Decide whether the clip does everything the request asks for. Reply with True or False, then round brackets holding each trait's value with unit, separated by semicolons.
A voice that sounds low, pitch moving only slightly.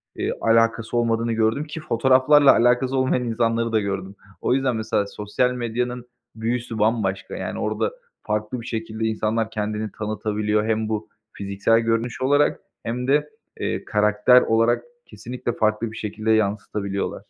True (115 Hz; 2.3 semitones)